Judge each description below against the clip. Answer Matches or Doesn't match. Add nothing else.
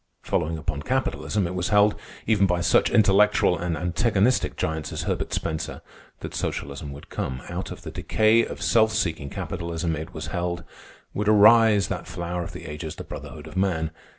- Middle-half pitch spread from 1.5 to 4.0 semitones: Doesn't match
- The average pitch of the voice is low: Matches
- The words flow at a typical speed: Matches